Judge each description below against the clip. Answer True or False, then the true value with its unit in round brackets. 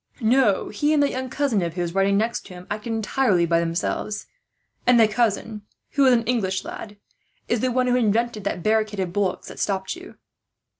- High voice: True (215 Hz)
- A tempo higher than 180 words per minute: True (200 wpm)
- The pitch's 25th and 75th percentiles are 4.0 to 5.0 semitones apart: True (4.3 semitones)